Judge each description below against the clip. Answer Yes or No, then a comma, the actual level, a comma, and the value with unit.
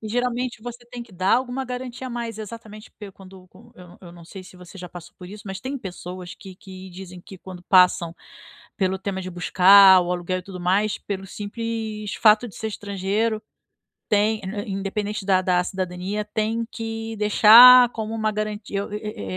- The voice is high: Yes, high, 205 Hz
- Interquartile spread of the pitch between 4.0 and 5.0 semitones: No, average, 3.2 semitones